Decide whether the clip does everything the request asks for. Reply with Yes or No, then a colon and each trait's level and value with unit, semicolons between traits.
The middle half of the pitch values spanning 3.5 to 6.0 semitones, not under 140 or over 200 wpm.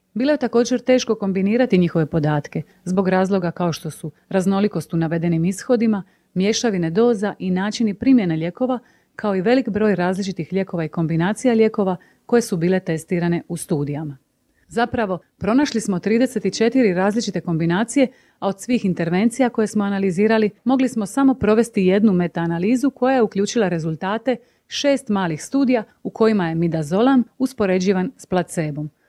Yes: average, 5.0 semitones; average, 145 wpm